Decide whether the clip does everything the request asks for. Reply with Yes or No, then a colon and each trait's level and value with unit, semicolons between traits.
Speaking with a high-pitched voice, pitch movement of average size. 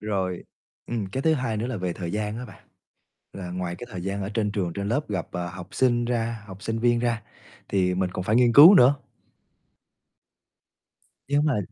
No: low, 105 Hz; average, 4.3 semitones